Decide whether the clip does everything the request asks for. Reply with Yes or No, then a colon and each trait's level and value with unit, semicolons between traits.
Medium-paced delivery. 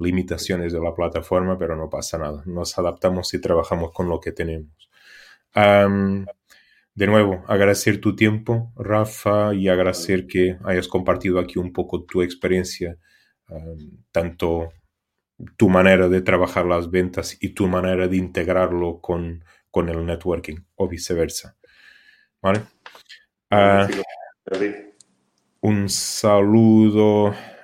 No: slow, 120 wpm